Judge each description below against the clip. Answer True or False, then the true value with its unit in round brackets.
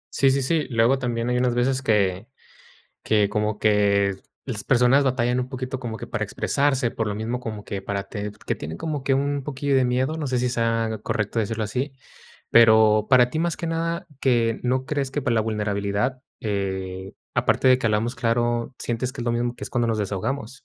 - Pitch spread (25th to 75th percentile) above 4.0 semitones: False (3.6 semitones)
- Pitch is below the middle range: True (120 Hz)